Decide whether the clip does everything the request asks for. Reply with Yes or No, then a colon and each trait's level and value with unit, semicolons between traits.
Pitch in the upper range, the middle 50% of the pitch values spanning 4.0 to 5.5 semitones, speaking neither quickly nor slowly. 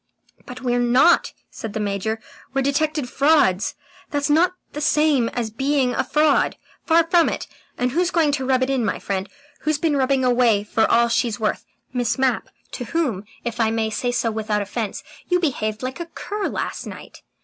Yes: very high, 255 Hz; average, 4.9 semitones; average, 190 wpm